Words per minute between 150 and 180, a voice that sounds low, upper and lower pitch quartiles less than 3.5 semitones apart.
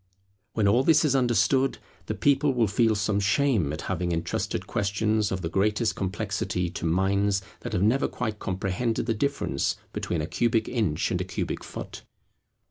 No: average, 170 wpm; low, 105 Hz; average, 4.0 semitones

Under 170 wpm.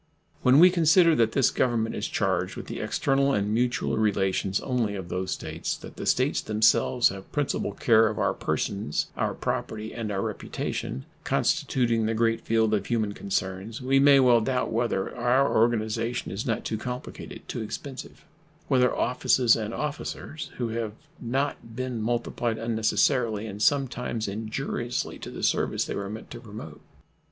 Yes: average, 160 wpm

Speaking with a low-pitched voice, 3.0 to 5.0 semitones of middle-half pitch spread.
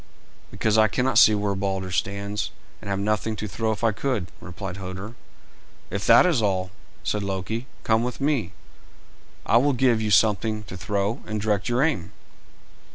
No: low, 105 Hz; narrow, 2.6 semitones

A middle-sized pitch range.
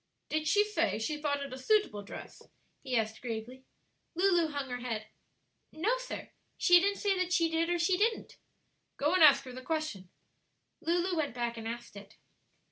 No: wide, 6.6 semitones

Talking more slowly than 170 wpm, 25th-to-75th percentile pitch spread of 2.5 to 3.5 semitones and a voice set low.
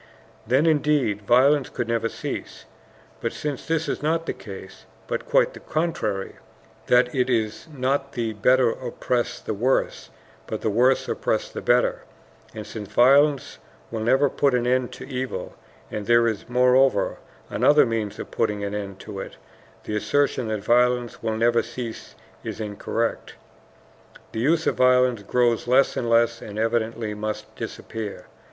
Yes: average, 160 wpm; average, 3.2 semitones; low, 120 Hz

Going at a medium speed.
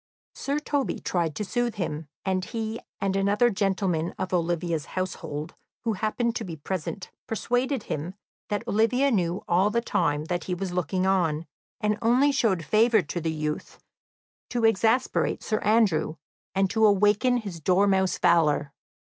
Yes: average, 155 wpm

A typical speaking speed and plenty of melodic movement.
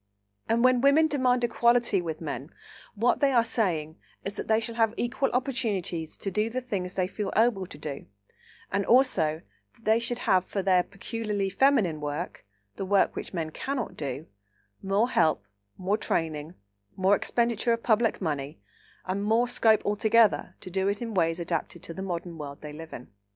Yes: average, 175 wpm; wide, 6.1 semitones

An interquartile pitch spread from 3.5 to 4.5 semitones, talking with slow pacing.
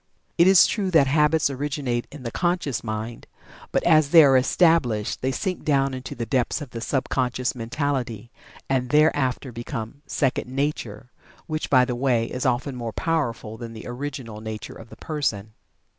No: average, 3.9 semitones; average, 175 wpm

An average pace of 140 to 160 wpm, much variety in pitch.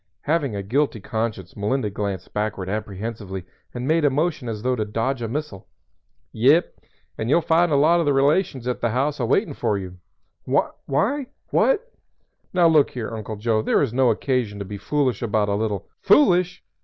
No: average, 190 wpm; wide, 5.9 semitones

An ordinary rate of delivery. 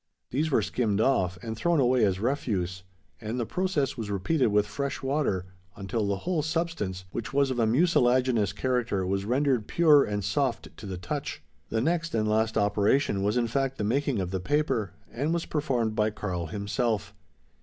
Yes: average, 185 wpm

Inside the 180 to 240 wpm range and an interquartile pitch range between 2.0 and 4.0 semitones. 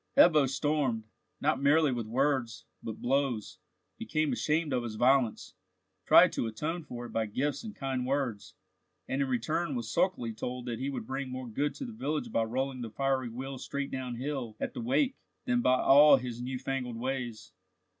Yes: average, 185 wpm; average, 3.1 semitones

